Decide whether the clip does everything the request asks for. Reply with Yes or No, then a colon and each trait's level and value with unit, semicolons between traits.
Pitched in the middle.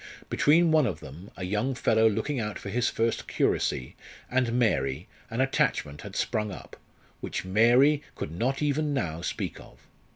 No: low, 115 Hz